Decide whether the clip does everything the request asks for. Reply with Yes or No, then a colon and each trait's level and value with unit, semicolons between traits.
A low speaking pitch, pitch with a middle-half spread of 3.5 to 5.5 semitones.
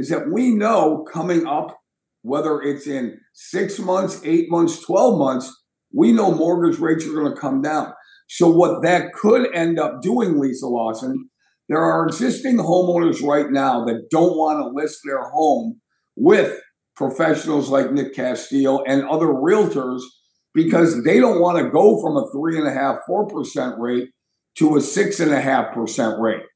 No: medium, 160 Hz; average, 4.2 semitones